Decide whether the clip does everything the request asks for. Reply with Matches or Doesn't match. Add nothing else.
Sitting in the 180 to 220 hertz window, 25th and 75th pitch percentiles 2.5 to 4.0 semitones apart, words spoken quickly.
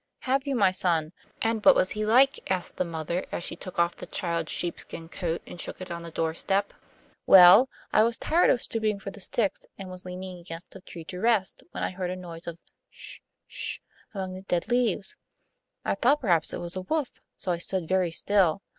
Matches